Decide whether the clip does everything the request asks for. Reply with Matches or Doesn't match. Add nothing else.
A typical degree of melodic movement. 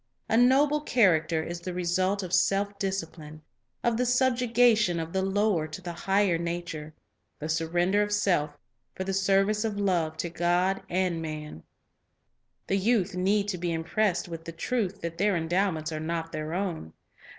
Matches